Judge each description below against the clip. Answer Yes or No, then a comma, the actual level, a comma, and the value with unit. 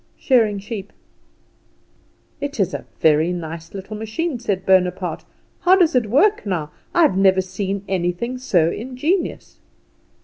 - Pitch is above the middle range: Yes, high, 200 Hz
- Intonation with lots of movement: Yes, wide, 5.8 semitones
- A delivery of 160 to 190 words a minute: No, slow, 135 wpm